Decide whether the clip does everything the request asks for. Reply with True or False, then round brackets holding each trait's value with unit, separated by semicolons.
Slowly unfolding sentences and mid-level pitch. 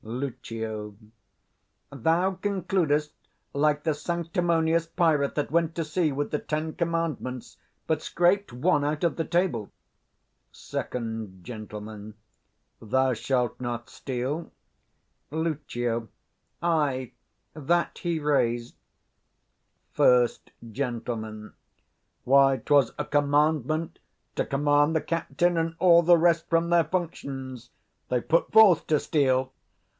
True (110 wpm; 150 Hz)